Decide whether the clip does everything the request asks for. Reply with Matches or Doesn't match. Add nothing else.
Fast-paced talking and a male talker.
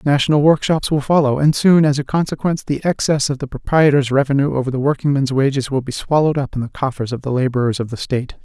Matches